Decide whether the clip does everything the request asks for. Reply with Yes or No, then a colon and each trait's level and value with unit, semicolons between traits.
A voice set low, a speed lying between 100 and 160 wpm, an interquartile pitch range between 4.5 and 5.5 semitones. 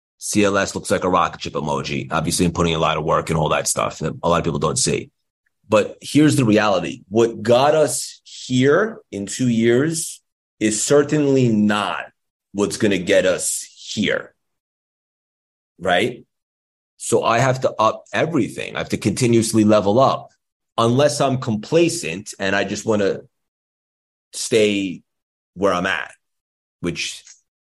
Yes: low, 105 Hz; average, 155 wpm; average, 5.0 semitones